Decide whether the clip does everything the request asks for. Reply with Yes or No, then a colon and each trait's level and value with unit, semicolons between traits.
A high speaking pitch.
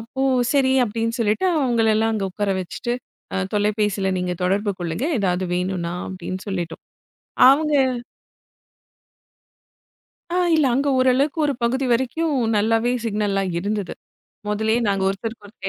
Yes: high, 210 Hz